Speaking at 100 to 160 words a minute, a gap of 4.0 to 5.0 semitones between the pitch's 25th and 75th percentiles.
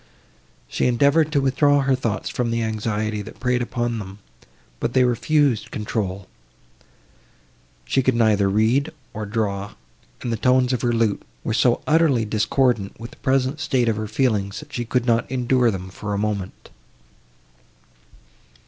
No: average, 155 wpm; average, 3.5 semitones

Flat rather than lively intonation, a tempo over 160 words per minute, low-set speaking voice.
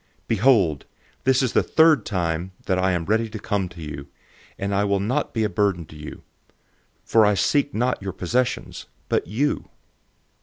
No: average, 4.5 semitones; average, 180 wpm; low, 100 Hz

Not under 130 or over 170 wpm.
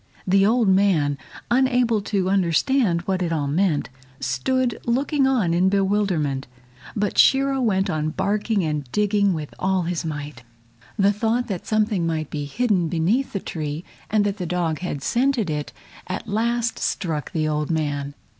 Yes: average, 160 wpm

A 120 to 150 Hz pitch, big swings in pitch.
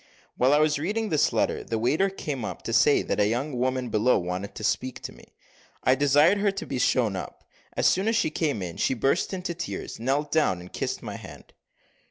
Yes: low, 135 Hz; wide, 5.9 semitones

